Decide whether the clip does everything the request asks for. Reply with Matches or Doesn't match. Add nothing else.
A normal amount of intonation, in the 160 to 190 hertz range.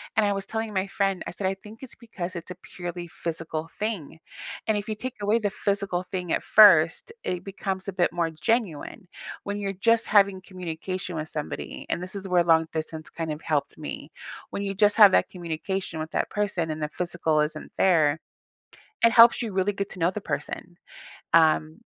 Matches